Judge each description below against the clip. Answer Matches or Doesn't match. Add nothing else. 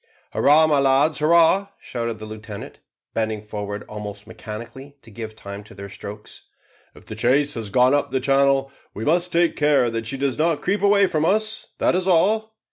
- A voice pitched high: Doesn't match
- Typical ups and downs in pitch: Doesn't match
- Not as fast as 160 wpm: Doesn't match